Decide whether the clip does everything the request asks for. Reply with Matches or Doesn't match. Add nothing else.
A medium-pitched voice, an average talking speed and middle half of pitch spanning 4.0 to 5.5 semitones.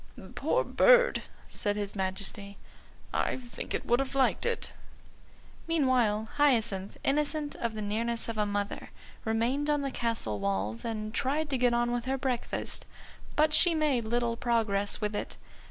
Doesn't match